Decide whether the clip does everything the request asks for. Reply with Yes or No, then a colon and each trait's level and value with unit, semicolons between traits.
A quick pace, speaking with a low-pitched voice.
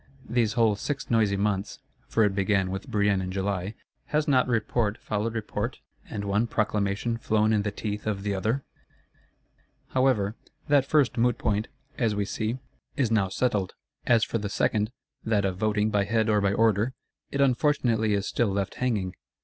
No: average, 175 wpm; low, 105 Hz